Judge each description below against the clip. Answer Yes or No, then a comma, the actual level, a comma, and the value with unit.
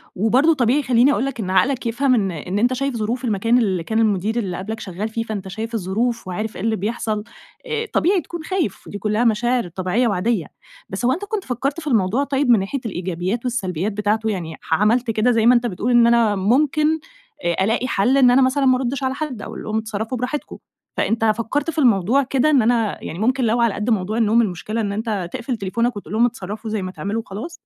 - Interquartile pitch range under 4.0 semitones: Yes, average, 3.6 semitones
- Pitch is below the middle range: No, high, 225 Hz